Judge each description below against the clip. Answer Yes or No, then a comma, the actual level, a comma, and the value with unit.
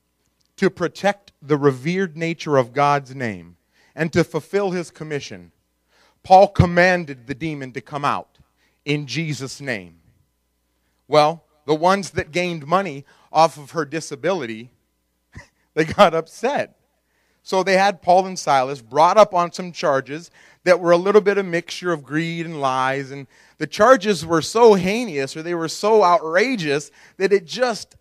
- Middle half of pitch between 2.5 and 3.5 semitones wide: No, average, 4.7 semitones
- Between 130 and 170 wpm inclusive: Yes, average, 155 wpm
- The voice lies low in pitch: No, medium, 160 Hz